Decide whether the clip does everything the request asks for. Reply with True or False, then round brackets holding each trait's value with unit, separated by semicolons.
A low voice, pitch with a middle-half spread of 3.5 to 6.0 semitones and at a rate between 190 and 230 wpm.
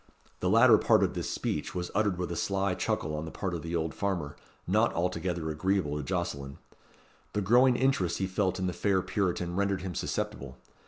False (90 Hz; 3.0 semitones; 200 wpm)